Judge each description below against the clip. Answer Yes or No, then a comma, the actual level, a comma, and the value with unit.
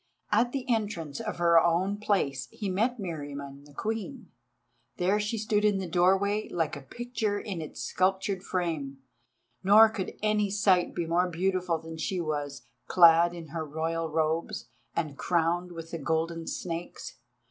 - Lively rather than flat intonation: No, average, 4.0 semitones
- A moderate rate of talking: Yes, average, 160 wpm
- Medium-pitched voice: Yes, medium, 175 Hz